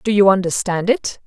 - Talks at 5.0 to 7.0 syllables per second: Yes, 5.1 syllables/s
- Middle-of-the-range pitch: No, high, 200 Hz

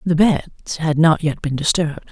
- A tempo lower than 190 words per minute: No, average, 200 wpm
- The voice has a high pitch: No, medium, 160 Hz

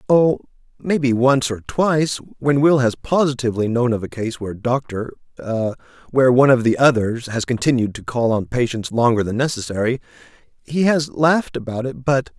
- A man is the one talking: Yes, male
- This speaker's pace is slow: No, average, 165 wpm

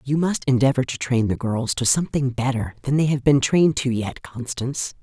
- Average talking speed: No, fast, 215 wpm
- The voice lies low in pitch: Yes, low, 130 Hz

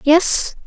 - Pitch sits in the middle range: No, very high, 330 Hz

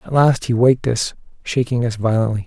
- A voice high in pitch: No, low, 120 Hz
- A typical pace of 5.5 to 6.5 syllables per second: Yes, 5.8 syllables/s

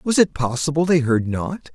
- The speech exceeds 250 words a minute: No, fast, 205 wpm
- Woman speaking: No, male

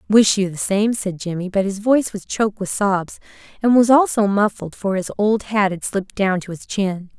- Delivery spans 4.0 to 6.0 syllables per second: Yes, 5.1 syllables/s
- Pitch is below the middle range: No, high, 200 Hz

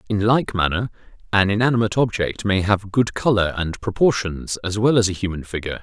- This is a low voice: Yes, low, 105 Hz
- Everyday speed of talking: Yes, average, 185 wpm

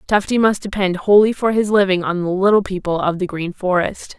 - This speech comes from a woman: Yes, female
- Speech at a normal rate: No, fast, 215 wpm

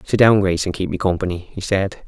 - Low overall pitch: Yes, very low, 95 Hz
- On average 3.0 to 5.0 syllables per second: No, 6.3 syllables/s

